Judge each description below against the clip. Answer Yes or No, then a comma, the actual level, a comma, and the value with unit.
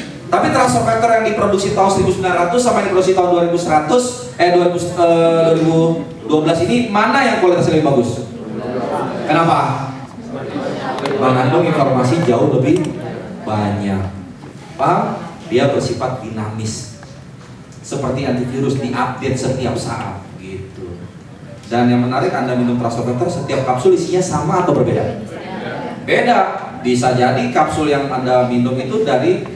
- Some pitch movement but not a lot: No, wide, 6.2 semitones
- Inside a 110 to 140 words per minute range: Yes, average, 120 wpm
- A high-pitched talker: No, medium, 140 Hz